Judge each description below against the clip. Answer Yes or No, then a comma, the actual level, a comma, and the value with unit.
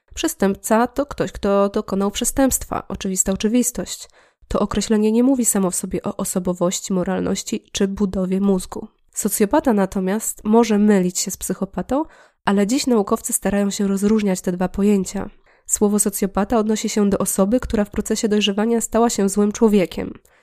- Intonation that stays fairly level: Yes, narrow, 2.3 semitones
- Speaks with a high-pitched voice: Yes, high, 205 Hz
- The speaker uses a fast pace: No, average, 150 wpm